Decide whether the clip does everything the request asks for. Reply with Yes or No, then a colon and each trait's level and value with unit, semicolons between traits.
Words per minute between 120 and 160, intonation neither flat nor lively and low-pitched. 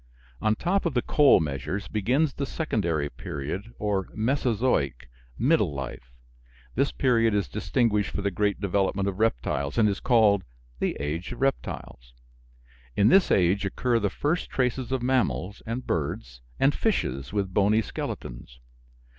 No: average, 145 wpm; wide, 6.1 semitones; low, 105 Hz